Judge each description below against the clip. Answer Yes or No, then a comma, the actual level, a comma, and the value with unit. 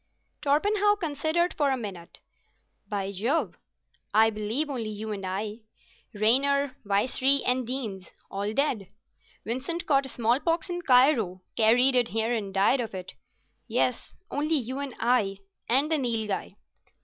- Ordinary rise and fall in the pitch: Yes, average, 5.0 semitones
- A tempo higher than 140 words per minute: No, slow, 135 wpm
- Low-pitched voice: No, high, 245 Hz